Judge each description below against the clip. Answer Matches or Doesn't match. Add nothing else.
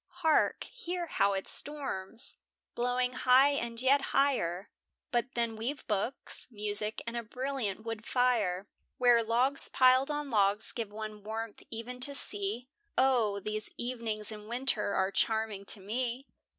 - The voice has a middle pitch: Doesn't match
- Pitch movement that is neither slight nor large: Matches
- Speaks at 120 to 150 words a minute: Matches